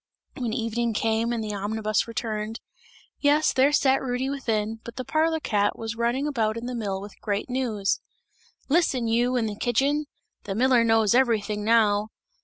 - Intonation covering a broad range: No, average, 3.1 semitones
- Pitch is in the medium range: No, high, 230 Hz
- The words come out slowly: No, average, 170 wpm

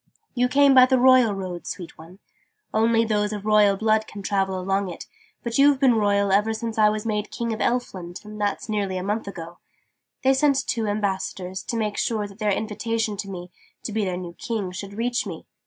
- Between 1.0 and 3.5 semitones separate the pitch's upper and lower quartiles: Yes, average, 2.8 semitones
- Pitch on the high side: Yes, high, 210 Hz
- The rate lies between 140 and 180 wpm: No, fast, 205 wpm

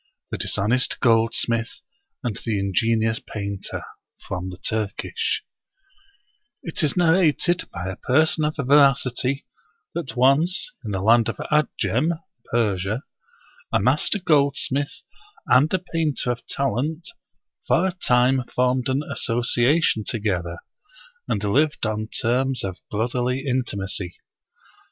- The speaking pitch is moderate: No, low, 125 Hz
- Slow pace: Yes, slow, 120 wpm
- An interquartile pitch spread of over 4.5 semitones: Yes, average, 5.2 semitones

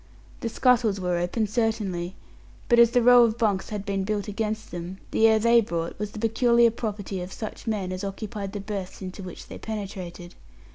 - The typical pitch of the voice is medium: No, high, 210 Hz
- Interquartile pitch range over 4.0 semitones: No, average, 3.0 semitones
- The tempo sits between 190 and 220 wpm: Yes, average, 195 wpm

